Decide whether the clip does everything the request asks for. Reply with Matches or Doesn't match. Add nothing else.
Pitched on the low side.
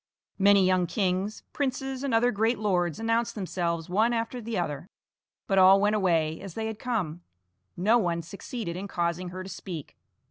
Doesn't match